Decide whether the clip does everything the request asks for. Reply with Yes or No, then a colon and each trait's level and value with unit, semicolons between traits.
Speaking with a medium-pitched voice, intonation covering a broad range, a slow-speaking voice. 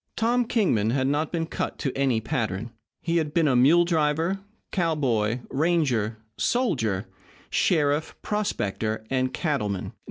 Yes: medium, 145 Hz; wide, 6.4 semitones; slow, 125 wpm